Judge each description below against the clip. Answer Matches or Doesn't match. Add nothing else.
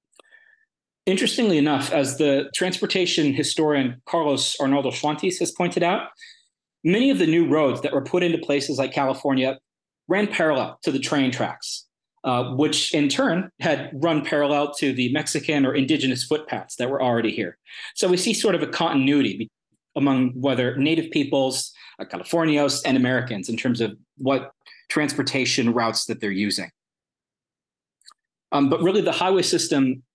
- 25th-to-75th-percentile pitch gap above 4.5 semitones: Doesn't match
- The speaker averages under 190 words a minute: Matches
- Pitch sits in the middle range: Matches